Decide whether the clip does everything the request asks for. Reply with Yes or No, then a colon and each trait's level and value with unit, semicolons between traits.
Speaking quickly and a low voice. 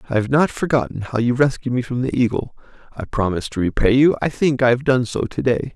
Yes: fast, 250 wpm; low, 125 Hz